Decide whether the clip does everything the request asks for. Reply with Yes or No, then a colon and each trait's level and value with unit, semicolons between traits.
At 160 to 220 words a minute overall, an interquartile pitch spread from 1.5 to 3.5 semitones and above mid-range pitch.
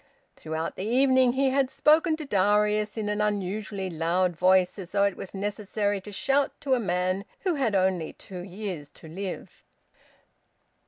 No: average, 165 wpm; average, 3.9 semitones; high, 200 Hz